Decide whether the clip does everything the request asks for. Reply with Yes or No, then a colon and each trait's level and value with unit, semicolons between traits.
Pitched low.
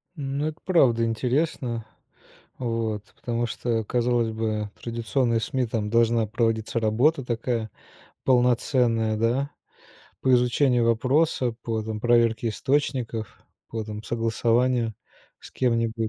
Yes: low, 115 Hz